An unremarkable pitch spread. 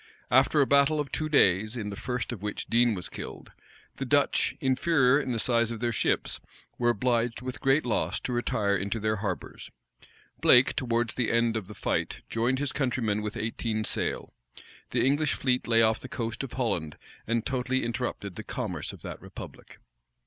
Yes: average, 3.1 semitones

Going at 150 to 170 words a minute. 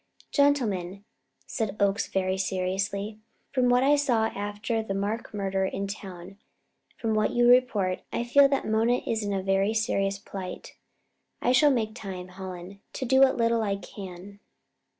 Yes: average, 165 wpm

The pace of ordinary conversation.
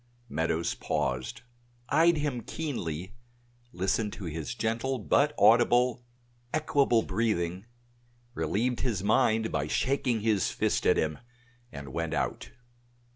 No: slow, 115 wpm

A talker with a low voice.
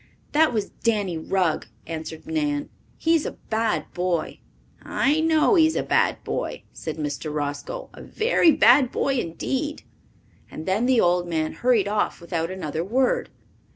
No: high, 215 Hz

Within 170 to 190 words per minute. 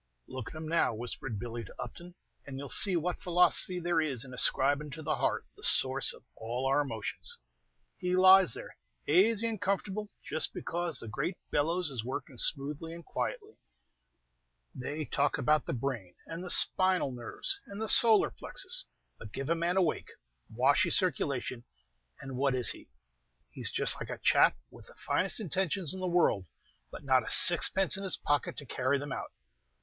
Yes: average, 185 wpm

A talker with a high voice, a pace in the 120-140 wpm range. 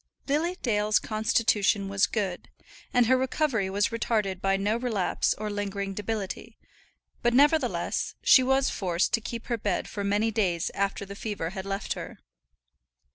No: high, 210 Hz; average, 155 wpm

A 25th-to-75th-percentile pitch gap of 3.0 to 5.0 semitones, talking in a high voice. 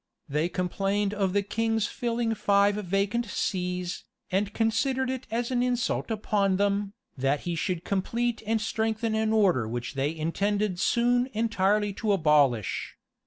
Yes: average, 3.6 semitones; high, 205 Hz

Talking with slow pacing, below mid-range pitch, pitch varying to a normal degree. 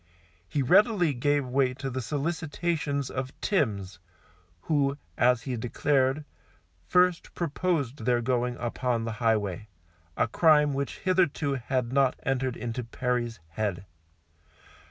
Yes: slow, 120 wpm; low, 130 Hz; average, 3.5 semitones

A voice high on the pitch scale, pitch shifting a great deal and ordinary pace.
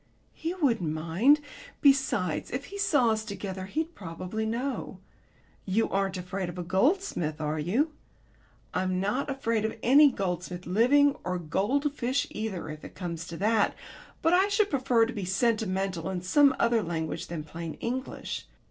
Yes: high, 210 Hz; wide, 6.9 semitones; average, 155 wpm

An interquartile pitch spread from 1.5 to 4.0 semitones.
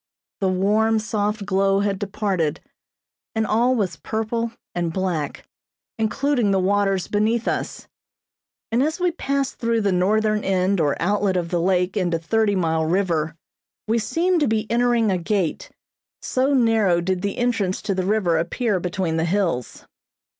Yes: average, 3.6 semitones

